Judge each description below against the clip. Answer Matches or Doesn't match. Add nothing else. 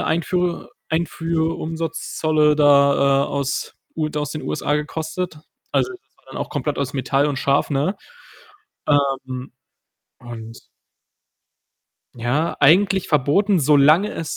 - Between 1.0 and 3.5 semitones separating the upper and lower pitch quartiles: Matches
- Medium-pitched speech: Matches